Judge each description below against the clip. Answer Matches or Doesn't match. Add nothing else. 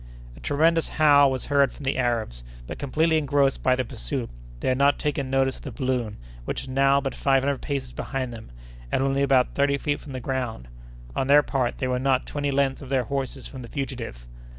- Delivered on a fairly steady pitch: Matches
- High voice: Doesn't match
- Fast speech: Matches